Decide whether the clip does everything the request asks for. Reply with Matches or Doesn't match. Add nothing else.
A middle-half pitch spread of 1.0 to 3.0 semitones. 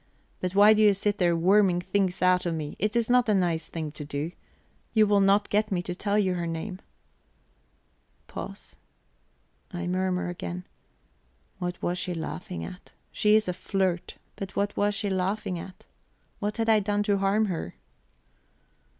Matches